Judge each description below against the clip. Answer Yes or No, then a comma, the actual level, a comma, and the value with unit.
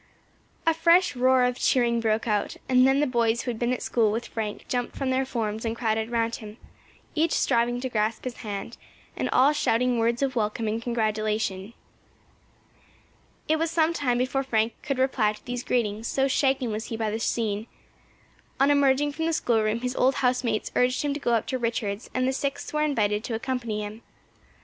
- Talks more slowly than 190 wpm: No, average, 200 wpm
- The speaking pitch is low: No, high, 240 Hz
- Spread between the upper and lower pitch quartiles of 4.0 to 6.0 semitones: No, average, 3.0 semitones